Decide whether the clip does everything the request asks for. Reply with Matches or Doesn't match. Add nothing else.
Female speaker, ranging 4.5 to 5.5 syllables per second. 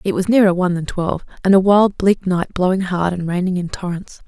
Doesn't match